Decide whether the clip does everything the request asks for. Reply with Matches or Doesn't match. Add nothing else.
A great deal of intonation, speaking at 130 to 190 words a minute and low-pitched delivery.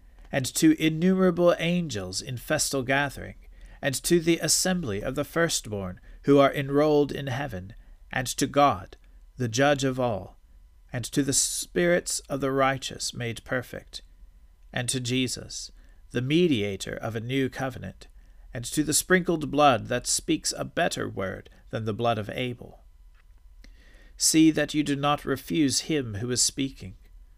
Matches